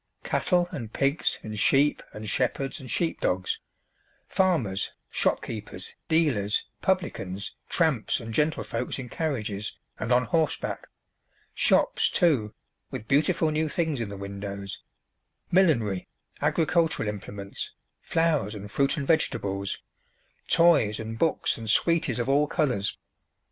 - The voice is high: No, low, 125 Hz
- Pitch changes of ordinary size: No, wide, 7.3 semitones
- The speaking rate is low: Yes, slow, 115 wpm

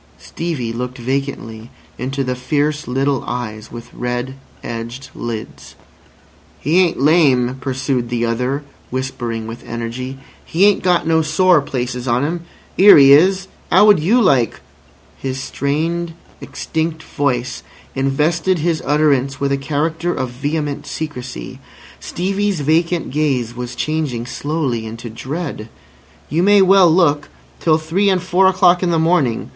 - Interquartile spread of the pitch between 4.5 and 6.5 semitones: Yes, average, 5.0 semitones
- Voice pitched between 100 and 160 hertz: Yes, medium, 140 Hz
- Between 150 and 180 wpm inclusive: No, average, 140 wpm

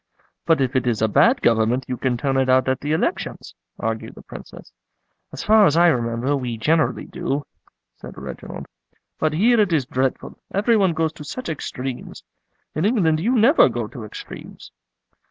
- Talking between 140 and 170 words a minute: No, average, 180 wpm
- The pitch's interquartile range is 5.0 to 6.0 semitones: Yes, wide, 5.6 semitones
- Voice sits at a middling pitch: Yes, medium, 145 Hz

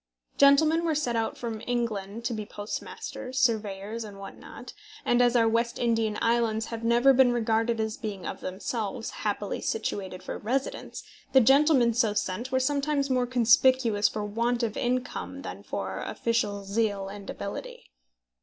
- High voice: Yes, high, 230 Hz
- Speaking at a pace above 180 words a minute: No, average, 160 wpm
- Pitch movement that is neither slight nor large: Yes, average, 3.0 semitones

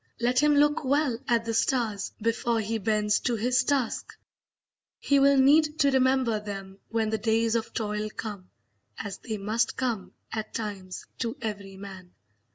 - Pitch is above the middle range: Yes, high, 225 Hz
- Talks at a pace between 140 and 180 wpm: Yes, average, 165 wpm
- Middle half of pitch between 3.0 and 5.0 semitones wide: Yes, average, 3.6 semitones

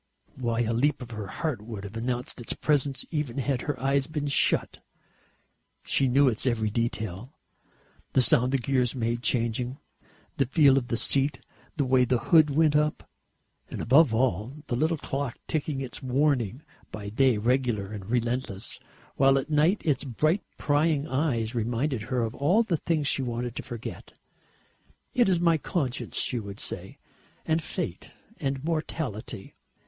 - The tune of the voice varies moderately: Yes, average, 3.9 semitones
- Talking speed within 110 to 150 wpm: No, average, 165 wpm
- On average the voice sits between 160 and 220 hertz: No, low, 130 Hz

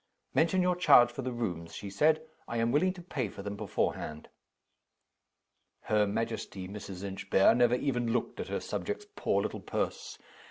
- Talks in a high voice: No, low, 115 Hz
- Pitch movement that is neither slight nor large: No, wide, 5.7 semitones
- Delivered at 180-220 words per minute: No, average, 165 wpm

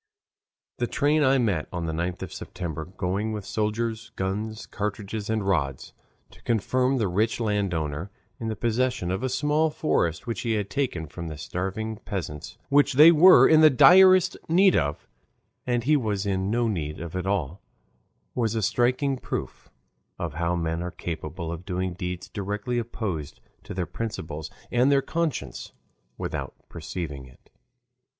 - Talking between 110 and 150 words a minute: No, average, 160 wpm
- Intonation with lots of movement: Yes, wide, 6.0 semitones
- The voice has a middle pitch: No, low, 105 Hz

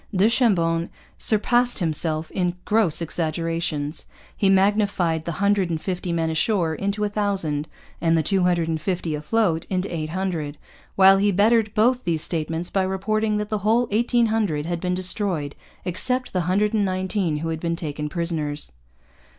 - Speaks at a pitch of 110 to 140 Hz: No, medium, 180 Hz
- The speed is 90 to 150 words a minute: No, average, 165 wpm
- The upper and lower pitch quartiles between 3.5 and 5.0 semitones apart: Yes, average, 4.0 semitones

